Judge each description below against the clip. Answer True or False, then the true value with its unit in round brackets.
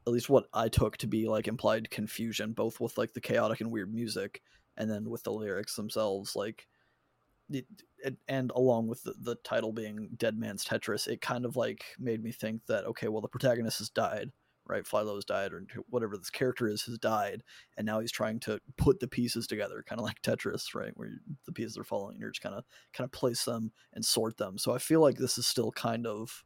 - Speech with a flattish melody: True (1.6 semitones)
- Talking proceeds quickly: True (235 wpm)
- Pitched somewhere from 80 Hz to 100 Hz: False (115 Hz)